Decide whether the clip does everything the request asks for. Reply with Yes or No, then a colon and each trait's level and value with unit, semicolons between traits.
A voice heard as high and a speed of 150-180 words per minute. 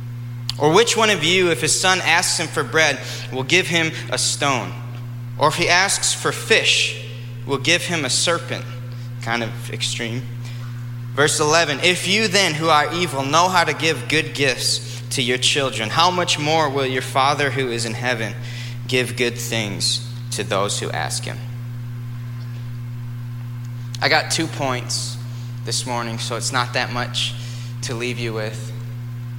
No: low, 120 Hz; average, 165 wpm